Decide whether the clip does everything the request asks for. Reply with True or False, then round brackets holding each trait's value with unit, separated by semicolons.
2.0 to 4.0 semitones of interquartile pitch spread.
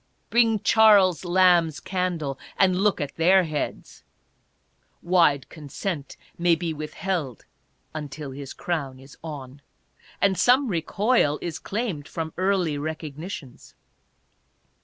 False (4.4 semitones)